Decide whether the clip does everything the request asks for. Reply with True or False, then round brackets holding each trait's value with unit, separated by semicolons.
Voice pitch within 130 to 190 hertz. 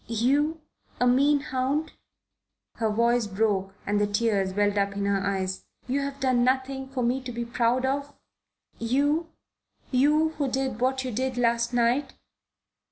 False (245 Hz)